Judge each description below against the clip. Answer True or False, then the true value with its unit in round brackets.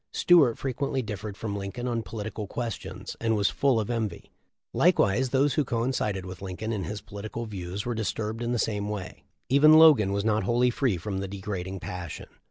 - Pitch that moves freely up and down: False (3.6 semitones)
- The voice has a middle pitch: False (110 Hz)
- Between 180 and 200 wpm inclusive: True (185 wpm)